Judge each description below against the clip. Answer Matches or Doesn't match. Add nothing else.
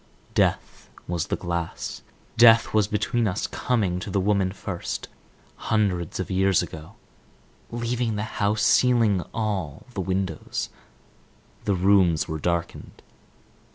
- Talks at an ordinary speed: Doesn't match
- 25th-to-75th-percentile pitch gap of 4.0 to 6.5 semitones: Doesn't match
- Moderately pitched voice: Doesn't match